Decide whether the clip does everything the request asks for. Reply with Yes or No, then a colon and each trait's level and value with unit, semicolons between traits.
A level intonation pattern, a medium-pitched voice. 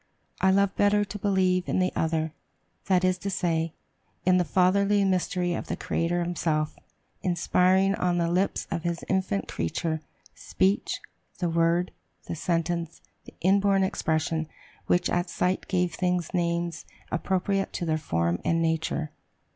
Yes: narrow, 2.2 semitones; medium, 175 Hz